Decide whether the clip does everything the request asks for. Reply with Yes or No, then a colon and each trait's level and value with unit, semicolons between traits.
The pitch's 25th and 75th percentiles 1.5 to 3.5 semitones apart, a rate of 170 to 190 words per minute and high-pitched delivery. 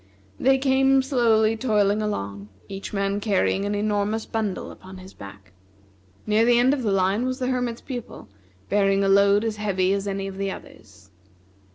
Yes: average, 3.0 semitones; average, 175 wpm; high, 205 Hz